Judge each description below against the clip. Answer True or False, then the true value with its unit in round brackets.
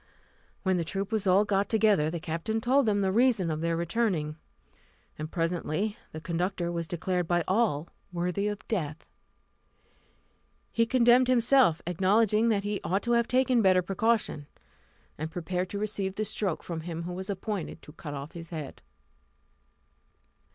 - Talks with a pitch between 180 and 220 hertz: True (190 Hz)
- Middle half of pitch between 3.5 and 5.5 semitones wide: True (4.5 semitones)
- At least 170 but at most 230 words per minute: False (160 wpm)